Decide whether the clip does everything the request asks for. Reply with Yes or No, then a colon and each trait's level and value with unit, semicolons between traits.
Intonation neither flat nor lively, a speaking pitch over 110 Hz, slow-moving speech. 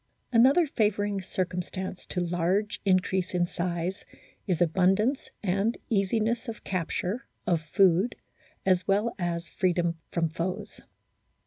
Yes: average, 3.0 semitones; medium, 185 Hz; slow, 115 wpm